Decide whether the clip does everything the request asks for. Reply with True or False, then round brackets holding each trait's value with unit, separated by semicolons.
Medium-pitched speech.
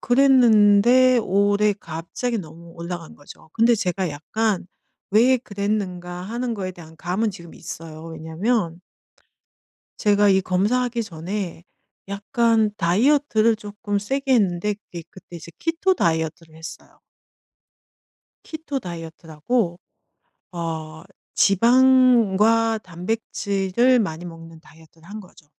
False (200 Hz)